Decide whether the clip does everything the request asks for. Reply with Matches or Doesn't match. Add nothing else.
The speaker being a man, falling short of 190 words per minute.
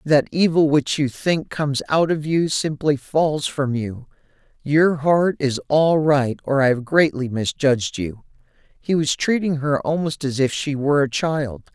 Matches